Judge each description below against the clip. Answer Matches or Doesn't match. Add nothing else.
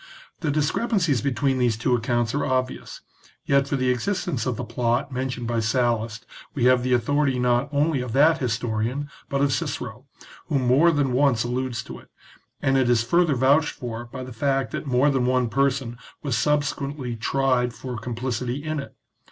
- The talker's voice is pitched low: Matches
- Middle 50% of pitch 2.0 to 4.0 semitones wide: Matches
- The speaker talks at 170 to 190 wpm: Matches